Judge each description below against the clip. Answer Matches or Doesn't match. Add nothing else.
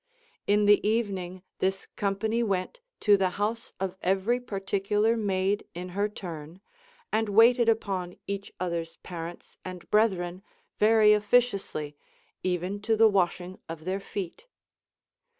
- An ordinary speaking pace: Doesn't match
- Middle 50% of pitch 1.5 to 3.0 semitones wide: Matches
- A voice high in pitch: Matches